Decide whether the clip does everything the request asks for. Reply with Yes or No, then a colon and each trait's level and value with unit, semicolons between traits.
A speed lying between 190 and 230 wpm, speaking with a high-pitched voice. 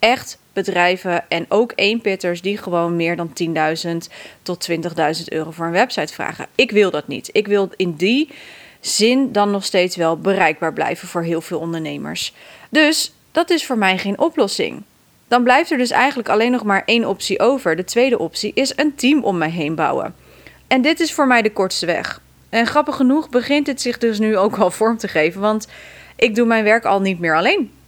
Yes: fast, 200 wpm; high, 200 Hz